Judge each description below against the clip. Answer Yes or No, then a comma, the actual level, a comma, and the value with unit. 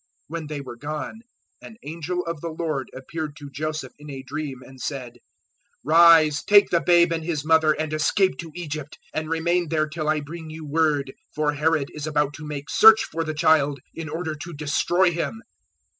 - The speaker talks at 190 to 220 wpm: Yes, average, 195 wpm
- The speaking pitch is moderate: Yes, medium, 155 Hz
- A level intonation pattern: Yes, narrow, 2.1 semitones